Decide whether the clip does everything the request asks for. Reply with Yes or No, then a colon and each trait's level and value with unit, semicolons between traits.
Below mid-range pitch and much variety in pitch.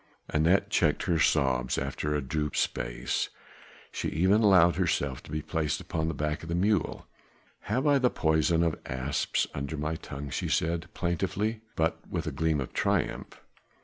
No: very low, 80 Hz; average, 2.9 semitones